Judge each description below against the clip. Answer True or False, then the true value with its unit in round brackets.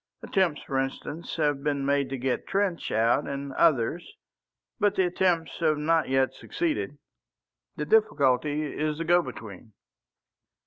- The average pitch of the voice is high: False (150 Hz)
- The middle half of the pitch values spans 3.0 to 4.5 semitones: True (4.1 semitones)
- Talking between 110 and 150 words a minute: True (140 wpm)